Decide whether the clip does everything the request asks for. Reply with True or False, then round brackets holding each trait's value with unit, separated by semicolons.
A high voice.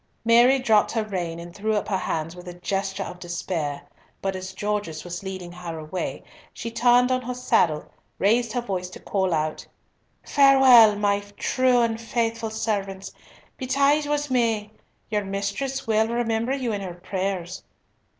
True (210 Hz)